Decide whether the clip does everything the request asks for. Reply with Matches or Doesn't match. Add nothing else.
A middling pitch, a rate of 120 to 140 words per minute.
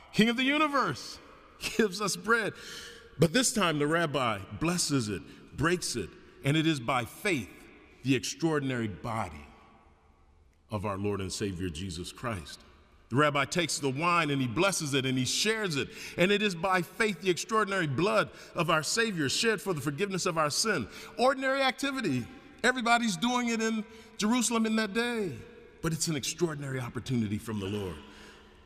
Doesn't match